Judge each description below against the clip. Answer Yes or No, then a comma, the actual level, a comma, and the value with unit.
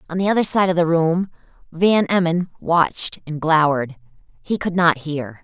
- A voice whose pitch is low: No, medium, 165 Hz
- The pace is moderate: Yes, average, 175 wpm